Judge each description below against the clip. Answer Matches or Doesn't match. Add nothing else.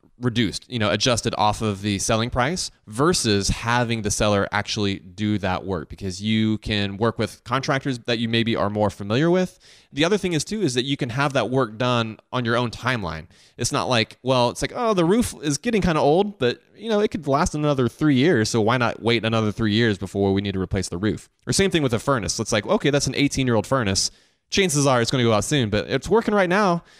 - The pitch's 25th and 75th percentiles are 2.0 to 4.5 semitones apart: Doesn't match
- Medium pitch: Doesn't match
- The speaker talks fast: Matches